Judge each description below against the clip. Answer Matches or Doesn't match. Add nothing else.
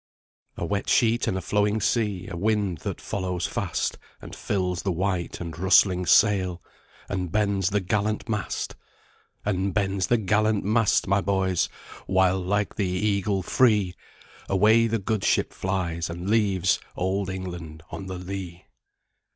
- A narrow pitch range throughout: Matches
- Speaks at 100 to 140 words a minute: Doesn't match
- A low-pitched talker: Matches